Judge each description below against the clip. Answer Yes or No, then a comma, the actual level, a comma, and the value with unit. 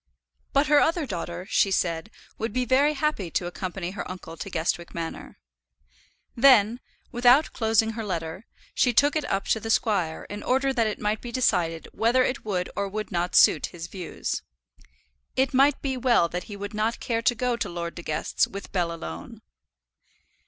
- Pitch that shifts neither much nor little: No, wide, 6.0 semitones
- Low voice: No, high, 210 Hz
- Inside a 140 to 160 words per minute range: No, average, 185 wpm